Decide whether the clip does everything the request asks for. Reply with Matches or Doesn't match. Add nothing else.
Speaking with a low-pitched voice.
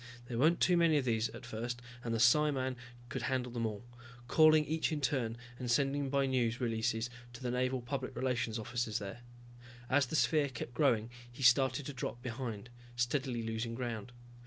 Matches